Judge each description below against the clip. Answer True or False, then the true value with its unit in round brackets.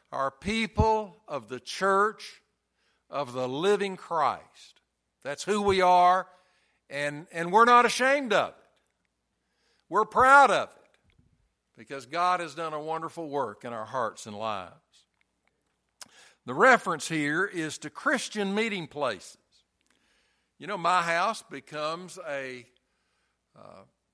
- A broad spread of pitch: True (6.7 semitones)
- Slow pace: True (125 wpm)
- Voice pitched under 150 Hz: False (170 Hz)